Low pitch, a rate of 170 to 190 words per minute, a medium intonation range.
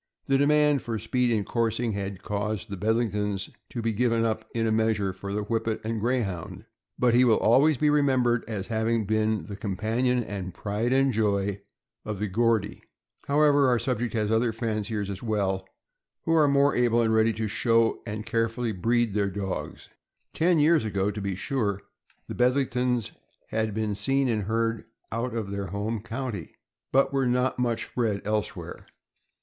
Yes: low, 115 Hz; average, 175 wpm; average, 3.1 semitones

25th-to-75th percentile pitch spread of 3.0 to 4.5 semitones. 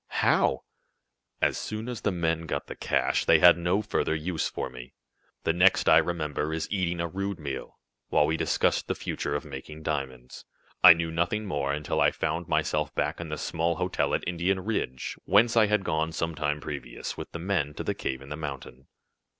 Yes: average, 3.3 semitones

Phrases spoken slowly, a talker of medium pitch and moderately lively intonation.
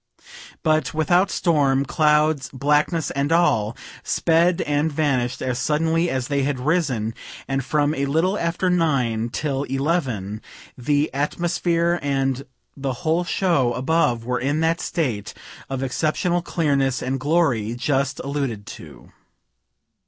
Yes: slow, 130 wpm; medium, 145 Hz; average, 3.8 semitones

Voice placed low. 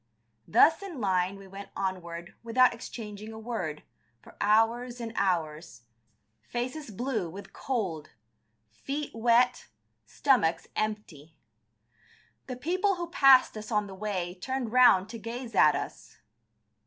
No: high, 220 Hz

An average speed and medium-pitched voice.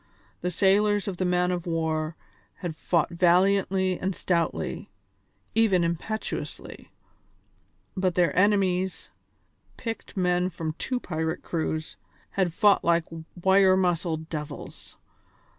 No: slow, 110 wpm; medium, 180 Hz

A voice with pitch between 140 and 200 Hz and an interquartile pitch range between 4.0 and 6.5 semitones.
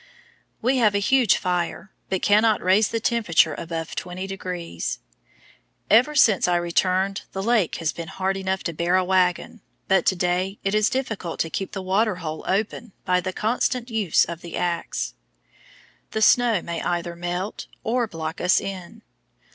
No: high, 190 Hz; average, 3.5 semitones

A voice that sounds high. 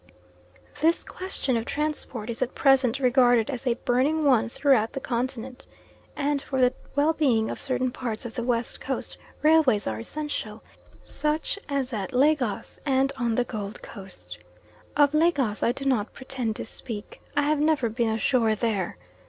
Yes: very high, 255 Hz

